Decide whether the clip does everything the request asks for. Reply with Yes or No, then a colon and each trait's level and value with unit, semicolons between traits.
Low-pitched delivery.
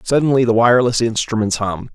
Yes: low, 115 Hz